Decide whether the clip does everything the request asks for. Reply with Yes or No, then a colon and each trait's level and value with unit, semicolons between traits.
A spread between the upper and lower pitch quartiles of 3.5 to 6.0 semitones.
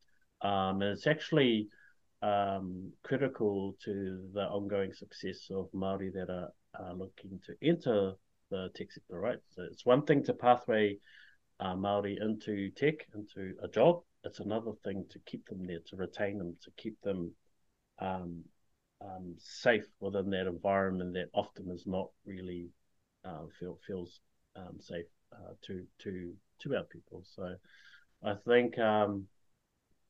No: narrow, 2.4 semitones